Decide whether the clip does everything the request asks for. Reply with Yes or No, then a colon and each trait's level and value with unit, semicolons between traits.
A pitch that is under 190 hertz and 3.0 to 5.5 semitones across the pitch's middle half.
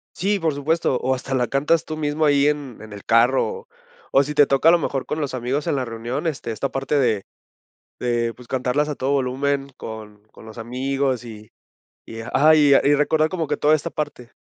Yes: low, 135 Hz; average, 3.4 semitones